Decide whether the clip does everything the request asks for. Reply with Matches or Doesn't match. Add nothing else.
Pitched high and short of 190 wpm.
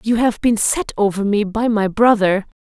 Doesn't match